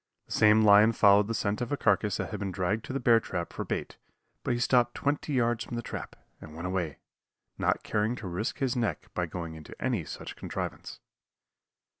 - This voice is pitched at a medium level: No, low, 105 Hz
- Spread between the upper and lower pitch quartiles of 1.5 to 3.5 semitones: No, average, 4.3 semitones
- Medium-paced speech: No, fast, 210 wpm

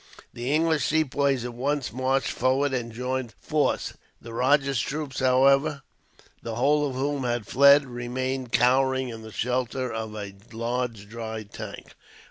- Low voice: Yes, low, 130 Hz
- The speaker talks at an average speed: Yes, average, 150 wpm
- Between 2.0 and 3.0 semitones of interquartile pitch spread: Yes, average, 2.7 semitones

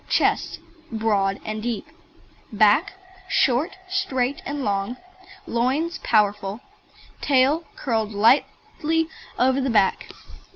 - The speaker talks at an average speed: No, slow, 95 wpm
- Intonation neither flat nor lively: Yes, average, 5.0 semitones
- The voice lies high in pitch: Yes, high, 240 Hz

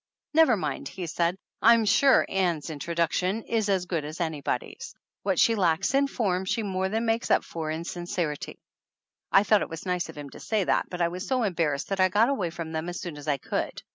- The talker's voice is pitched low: No, medium, 180 Hz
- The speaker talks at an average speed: No, fast, 250 wpm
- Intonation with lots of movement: No, average, 4.2 semitones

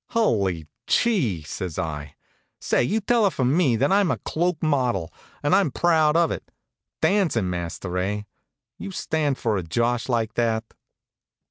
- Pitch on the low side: Yes, low, 125 Hz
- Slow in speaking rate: No, average, 155 wpm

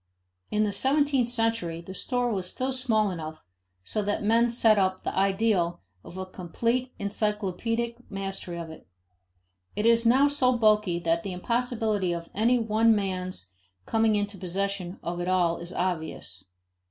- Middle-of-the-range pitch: No, high, 205 Hz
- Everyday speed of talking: Yes, average, 155 wpm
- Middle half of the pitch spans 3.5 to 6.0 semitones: Yes, average, 4.2 semitones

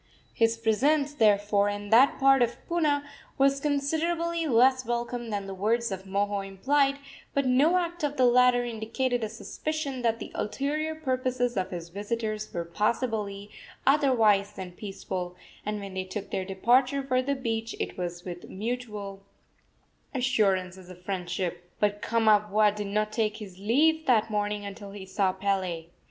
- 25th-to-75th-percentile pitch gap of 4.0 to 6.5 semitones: Yes, average, 4.7 semitones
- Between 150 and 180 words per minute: Yes, average, 155 wpm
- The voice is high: Yes, high, 220 Hz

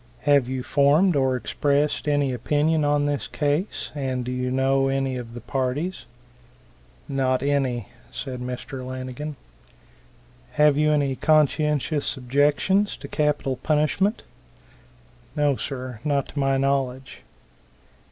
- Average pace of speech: No, slow, 125 wpm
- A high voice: No, medium, 140 Hz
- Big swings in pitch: No, narrow, 2.4 semitones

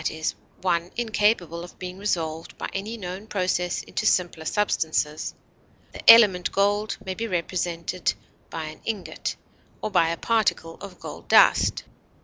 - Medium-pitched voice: Yes, medium, 180 Hz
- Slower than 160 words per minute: Yes, average, 140 wpm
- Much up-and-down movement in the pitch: No, average, 3.6 semitones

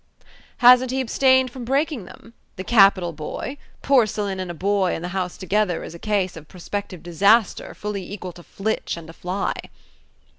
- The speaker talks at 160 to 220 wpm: Yes, average, 175 wpm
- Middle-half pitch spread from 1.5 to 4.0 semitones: No, average, 4.7 semitones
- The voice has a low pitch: No, high, 200 Hz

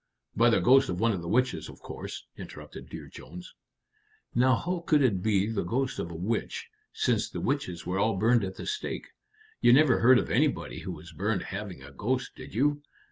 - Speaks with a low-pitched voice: Yes, low, 115 Hz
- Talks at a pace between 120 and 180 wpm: No, fast, 205 wpm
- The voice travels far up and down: Yes, wide, 6.1 semitones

